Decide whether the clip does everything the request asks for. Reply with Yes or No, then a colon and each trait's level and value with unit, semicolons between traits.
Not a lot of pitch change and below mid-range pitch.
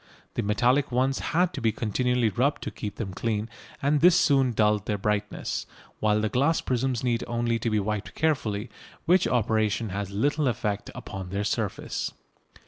No: average, 3.9 semitones; low, 115 Hz